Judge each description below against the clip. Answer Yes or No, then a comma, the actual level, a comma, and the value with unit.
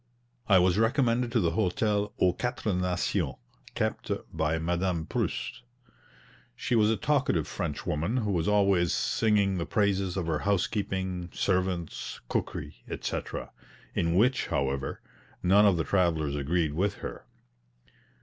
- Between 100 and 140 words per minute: Yes, slow, 135 wpm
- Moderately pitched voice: No, very low, 95 Hz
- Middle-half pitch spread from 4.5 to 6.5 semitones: No, average, 3.6 semitones